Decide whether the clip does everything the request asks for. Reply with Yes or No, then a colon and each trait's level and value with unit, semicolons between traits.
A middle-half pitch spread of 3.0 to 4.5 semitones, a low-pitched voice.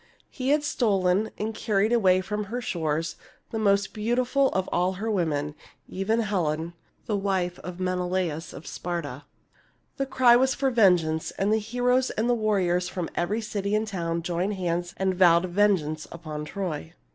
No: average, 4.0 semitones; high, 190 Hz